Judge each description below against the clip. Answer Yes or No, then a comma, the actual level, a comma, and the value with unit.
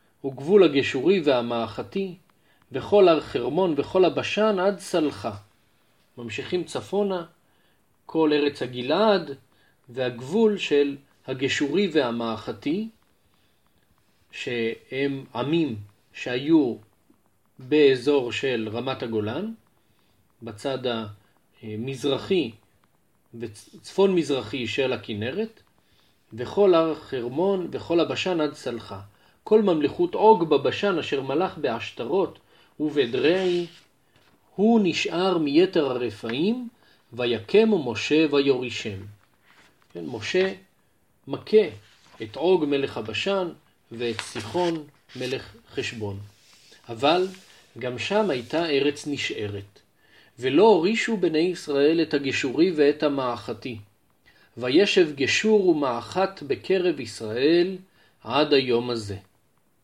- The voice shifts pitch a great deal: Yes, wide, 7.9 semitones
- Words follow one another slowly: Yes, slow, 85 wpm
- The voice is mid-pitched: Yes, medium, 145 Hz